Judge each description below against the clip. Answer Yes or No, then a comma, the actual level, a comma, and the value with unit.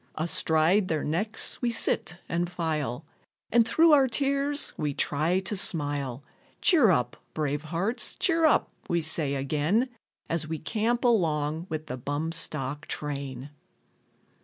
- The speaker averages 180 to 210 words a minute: No, slow, 135 wpm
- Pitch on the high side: No, medium, 160 Hz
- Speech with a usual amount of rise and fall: No, wide, 6.8 semitones